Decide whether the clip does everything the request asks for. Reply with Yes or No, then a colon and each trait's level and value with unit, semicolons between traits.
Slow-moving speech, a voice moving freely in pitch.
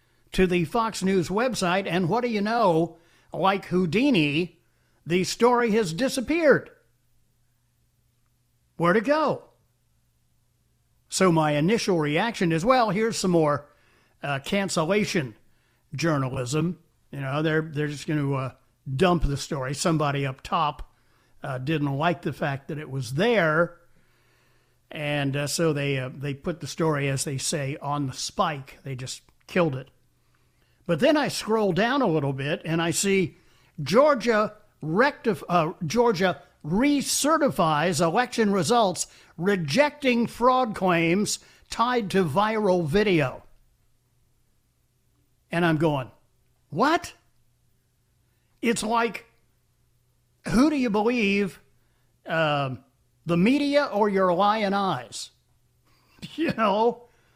Yes: slow, 120 wpm; wide, 7.7 semitones